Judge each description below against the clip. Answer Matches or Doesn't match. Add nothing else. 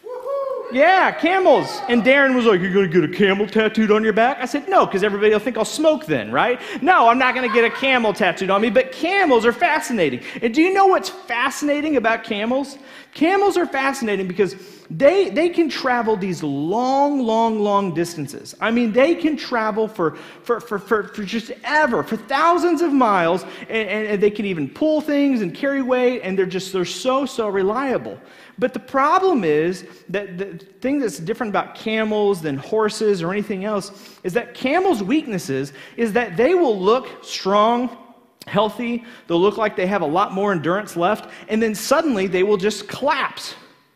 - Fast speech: Doesn't match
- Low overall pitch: Doesn't match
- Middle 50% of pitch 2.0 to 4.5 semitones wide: Doesn't match